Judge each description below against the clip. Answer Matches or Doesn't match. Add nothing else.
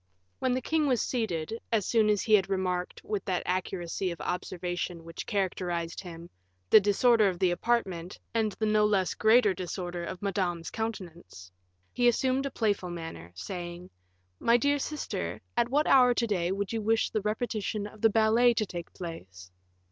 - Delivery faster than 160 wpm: Matches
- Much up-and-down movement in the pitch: Doesn't match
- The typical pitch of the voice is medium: Doesn't match